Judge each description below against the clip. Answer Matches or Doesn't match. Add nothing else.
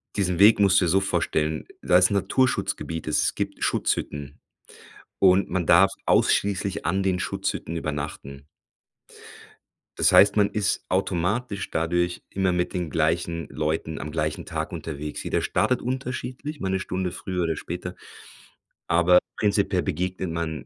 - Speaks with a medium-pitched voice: Doesn't match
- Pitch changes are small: Doesn't match